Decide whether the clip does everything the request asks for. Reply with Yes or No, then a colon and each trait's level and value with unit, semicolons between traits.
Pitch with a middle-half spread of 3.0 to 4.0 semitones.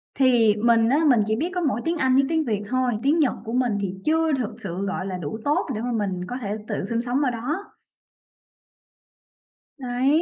No: average, 4.5 semitones